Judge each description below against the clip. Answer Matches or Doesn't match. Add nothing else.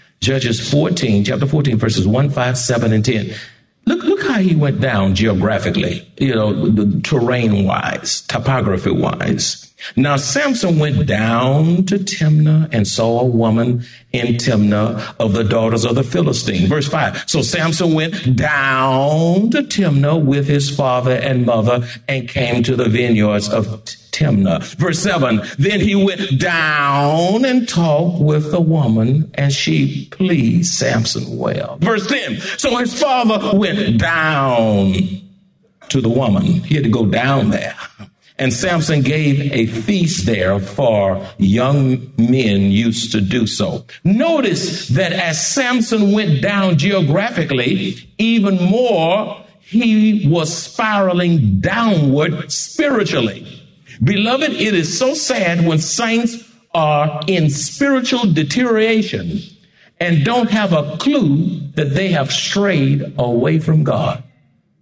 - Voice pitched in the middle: Matches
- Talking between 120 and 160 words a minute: Matches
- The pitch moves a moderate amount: Doesn't match